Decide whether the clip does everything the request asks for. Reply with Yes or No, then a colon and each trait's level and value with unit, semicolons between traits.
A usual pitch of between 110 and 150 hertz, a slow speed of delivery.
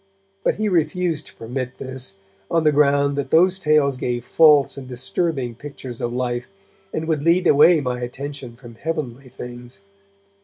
No: medium, 140 Hz; average, 160 wpm